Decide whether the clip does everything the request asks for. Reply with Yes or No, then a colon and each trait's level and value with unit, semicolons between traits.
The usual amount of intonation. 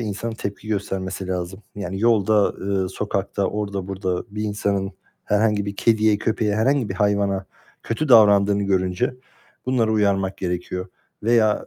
No: narrow, 2.0 semitones